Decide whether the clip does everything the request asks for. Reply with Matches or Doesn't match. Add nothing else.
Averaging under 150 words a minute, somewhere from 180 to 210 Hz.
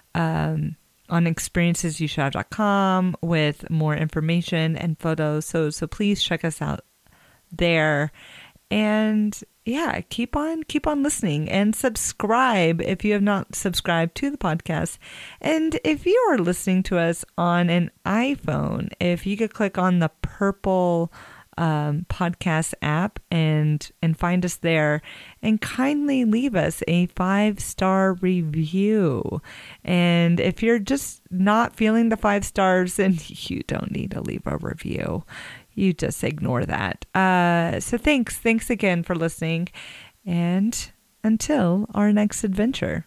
Matches